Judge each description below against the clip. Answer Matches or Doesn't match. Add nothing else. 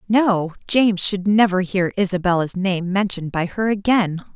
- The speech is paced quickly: Doesn't match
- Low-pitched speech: Doesn't match